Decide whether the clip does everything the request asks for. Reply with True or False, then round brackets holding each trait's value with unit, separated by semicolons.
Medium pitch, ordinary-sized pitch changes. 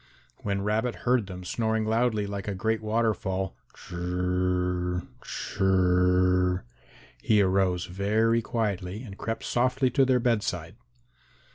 False (100 Hz; 3.7 semitones)